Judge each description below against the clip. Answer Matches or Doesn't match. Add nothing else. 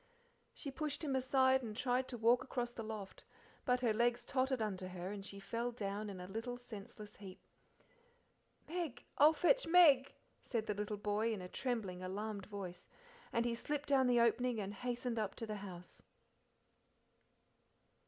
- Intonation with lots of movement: Doesn't match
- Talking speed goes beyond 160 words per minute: Matches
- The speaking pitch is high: Matches